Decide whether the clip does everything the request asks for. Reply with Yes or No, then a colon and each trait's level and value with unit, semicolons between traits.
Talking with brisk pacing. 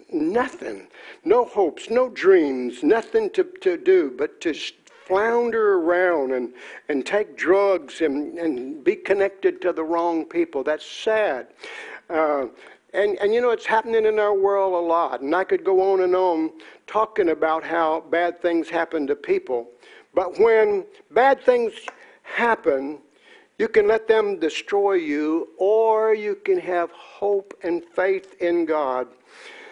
No: average, 150 wpm